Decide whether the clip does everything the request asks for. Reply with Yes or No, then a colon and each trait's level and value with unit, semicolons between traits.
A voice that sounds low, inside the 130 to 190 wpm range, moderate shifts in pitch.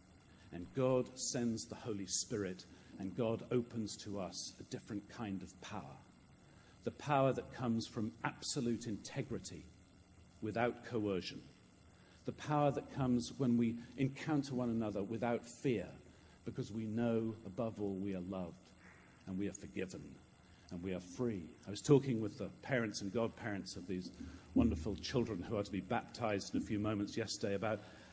Yes: low, 105 Hz; average, 160 wpm; average, 4.3 semitones